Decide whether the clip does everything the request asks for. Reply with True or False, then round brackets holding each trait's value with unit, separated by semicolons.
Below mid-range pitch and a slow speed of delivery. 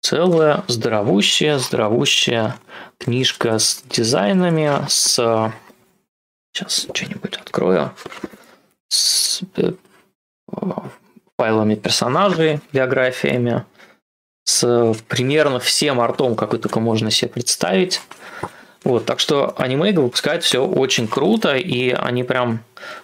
True (125 Hz; 90 wpm)